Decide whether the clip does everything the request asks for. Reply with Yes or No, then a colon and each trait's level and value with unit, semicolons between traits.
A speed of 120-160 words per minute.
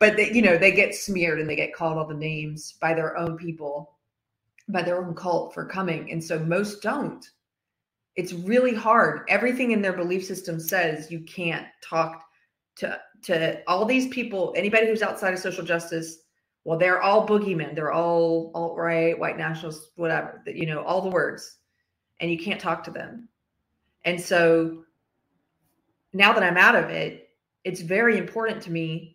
No: average, 180 wpm